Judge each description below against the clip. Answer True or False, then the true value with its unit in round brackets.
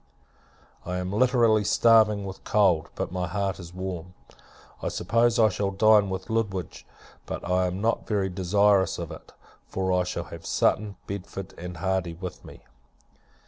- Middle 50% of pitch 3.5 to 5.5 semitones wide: False (2.5 semitones)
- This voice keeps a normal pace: True (160 wpm)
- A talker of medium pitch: False (95 Hz)